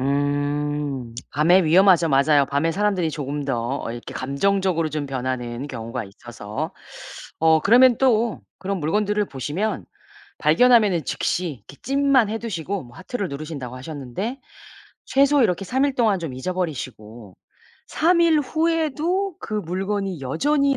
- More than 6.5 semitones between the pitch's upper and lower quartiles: Yes, wide, 7.9 semitones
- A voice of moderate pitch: Yes, medium, 170 Hz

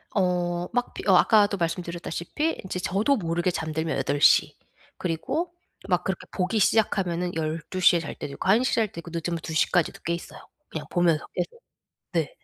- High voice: No, medium, 175 Hz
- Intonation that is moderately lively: Yes, average, 3.0 semitones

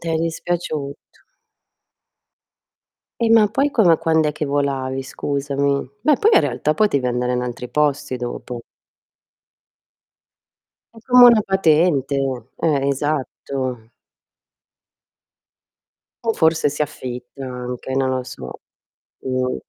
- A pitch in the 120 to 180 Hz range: Yes, medium, 140 Hz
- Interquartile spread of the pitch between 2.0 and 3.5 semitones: No, average, 4.2 semitones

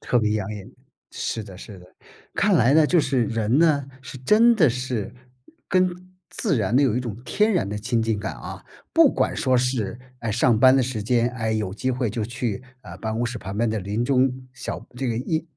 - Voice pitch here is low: Yes, low, 120 Hz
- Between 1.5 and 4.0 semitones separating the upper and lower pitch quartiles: Yes, average, 3.3 semitones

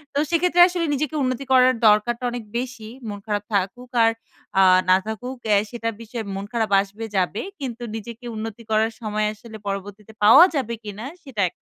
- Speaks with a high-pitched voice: Yes, high, 225 Hz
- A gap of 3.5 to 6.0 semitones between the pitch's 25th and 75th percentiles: No, average, 3.1 semitones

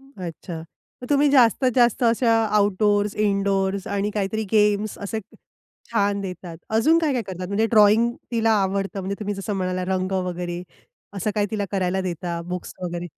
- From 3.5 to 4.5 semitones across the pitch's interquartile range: No, average, 2.9 semitones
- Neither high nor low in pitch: No, high, 200 Hz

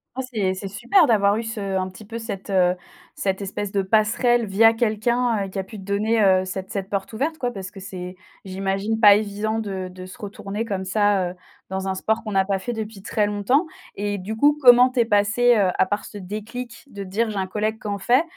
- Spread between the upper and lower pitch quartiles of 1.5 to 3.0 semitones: Yes, average, 2.7 semitones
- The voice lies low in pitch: No, high, 205 Hz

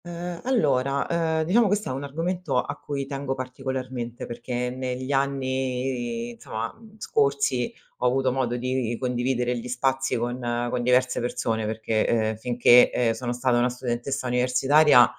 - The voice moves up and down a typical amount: No, narrow, 2.2 semitones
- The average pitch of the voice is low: Yes, low, 130 Hz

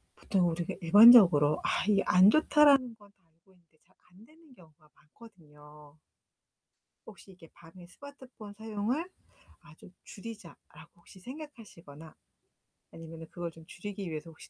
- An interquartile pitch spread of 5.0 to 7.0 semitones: Yes, wide, 5.4 semitones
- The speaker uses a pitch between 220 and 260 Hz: No, medium, 185 Hz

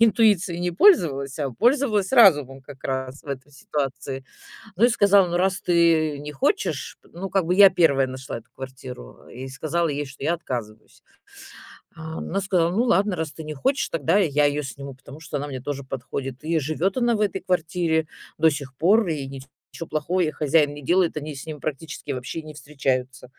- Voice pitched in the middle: Yes, medium, 155 Hz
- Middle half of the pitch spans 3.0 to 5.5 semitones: Yes, average, 4.8 semitones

